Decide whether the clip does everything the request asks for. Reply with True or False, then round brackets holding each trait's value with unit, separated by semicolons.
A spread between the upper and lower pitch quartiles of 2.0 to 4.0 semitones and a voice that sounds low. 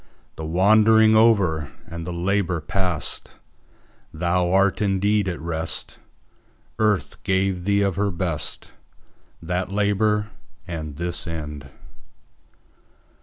True (3.3 semitones; 90 Hz)